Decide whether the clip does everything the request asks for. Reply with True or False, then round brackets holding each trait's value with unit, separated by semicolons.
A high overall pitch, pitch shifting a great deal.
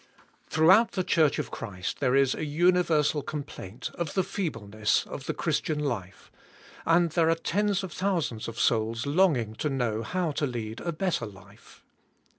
False (150 Hz; 7.1 semitones)